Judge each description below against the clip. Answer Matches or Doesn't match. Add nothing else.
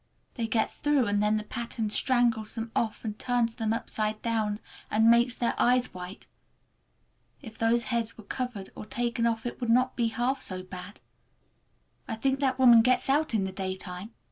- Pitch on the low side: Doesn't match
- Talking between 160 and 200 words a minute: Matches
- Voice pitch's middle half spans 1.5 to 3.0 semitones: Matches